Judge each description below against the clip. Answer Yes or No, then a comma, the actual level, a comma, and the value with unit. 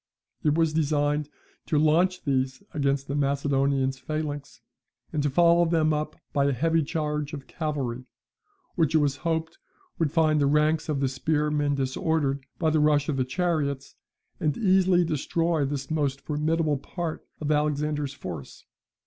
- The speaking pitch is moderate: Yes, medium, 150 Hz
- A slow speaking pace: No, average, 155 wpm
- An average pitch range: No, narrow, 2.3 semitones